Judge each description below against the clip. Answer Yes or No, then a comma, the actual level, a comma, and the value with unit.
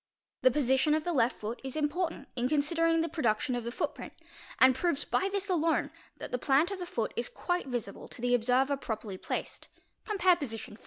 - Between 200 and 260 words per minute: Yes, fast, 205 wpm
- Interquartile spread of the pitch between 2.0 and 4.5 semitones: No, wide, 5.4 semitones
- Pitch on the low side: No, very high, 275 Hz